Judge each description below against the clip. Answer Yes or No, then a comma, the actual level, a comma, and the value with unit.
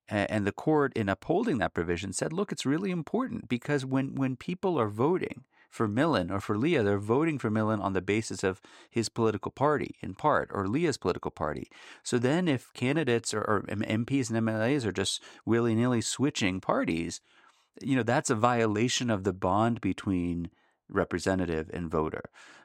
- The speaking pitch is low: Yes, low, 110 Hz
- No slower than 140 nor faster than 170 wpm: No, average, 180 wpm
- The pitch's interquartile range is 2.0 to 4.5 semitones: No, average, 5.3 semitones